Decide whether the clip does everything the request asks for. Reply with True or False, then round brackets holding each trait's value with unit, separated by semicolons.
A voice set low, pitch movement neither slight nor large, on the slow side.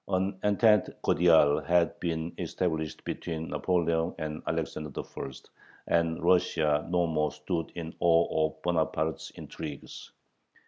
False (80 Hz; 2.0 semitones; 120 wpm)